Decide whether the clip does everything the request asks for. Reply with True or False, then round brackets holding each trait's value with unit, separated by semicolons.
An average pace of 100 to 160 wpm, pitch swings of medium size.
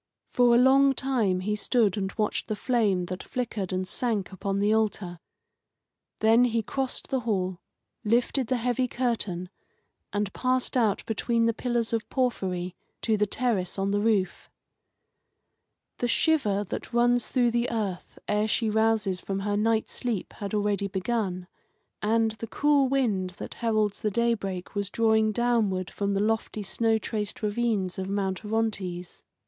True (155 wpm; 3.3 semitones)